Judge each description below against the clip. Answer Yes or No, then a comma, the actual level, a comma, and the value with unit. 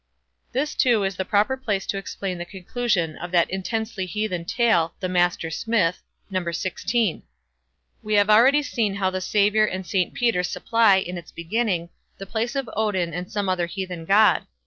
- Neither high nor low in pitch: No, high, 195 Hz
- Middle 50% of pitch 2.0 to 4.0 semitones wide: Yes, average, 3.6 semitones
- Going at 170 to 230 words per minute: Yes, average, 175 wpm